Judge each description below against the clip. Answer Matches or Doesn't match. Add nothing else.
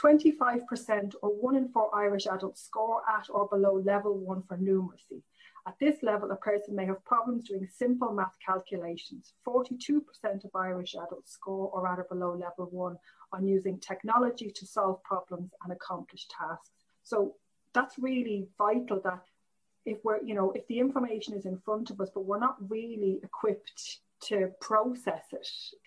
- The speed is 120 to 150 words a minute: Doesn't match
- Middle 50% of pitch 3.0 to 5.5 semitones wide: Matches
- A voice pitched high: Matches